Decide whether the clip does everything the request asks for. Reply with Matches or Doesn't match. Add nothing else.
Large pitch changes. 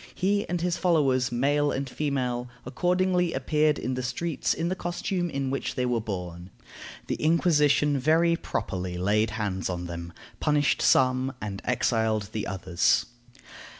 Matches